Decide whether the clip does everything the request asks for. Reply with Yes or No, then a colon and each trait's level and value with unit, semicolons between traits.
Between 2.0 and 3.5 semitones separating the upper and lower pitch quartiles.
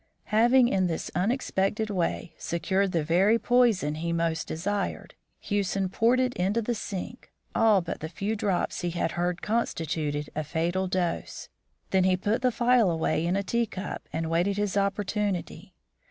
No: average, 4.0 semitones